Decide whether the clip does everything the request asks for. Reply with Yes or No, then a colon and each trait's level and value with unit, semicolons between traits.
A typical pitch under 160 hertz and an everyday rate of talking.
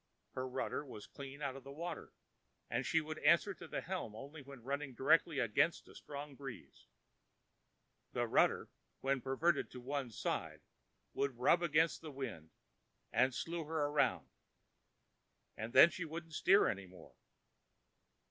Yes: medium, 140 Hz; average, 145 wpm